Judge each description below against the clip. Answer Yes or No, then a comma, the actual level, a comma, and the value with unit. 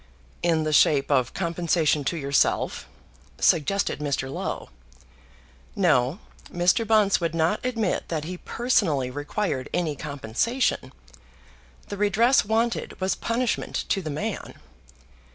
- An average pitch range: No, wide, 6.0 semitones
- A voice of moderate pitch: Yes, medium, 170 Hz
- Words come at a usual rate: No, slow, 115 wpm